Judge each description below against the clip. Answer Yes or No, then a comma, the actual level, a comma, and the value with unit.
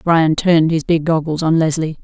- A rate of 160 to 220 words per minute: Yes, fast, 205 wpm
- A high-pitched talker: No, medium, 160 Hz